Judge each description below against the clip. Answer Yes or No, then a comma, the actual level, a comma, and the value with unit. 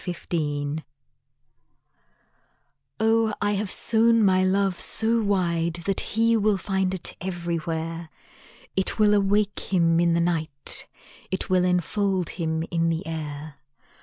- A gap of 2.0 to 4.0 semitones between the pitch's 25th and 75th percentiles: Yes, average, 3.5 semitones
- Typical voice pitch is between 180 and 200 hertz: Yes, medium, 185 Hz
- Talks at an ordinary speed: No, slow, 130 wpm